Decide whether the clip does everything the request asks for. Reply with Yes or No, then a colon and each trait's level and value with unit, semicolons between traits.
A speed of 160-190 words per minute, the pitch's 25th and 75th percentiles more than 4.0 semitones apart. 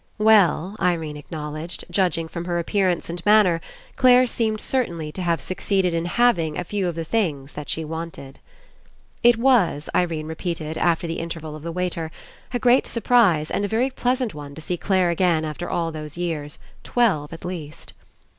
Yes: average, 180 wpm; average, 4.4 semitones